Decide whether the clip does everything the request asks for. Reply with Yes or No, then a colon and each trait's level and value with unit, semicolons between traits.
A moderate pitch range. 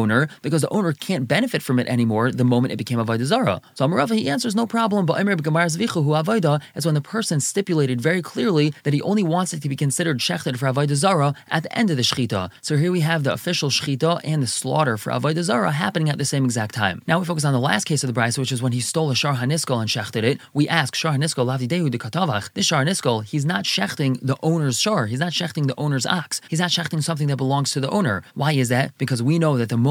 Yes: average, 4.5 semitones